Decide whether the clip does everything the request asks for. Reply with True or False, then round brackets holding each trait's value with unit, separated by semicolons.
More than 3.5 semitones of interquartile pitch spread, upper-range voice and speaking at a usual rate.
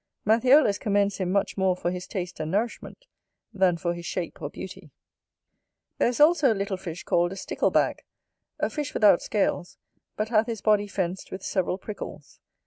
False (3.1 semitones; 195 Hz; 175 wpm)